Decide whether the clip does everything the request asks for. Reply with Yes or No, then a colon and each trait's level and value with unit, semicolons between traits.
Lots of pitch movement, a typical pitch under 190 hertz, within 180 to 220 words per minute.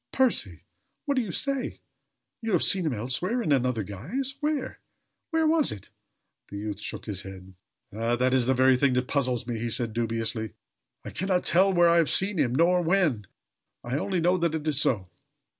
Yes: wide, 8.3 semitones; medium, 140 Hz; average, 200 wpm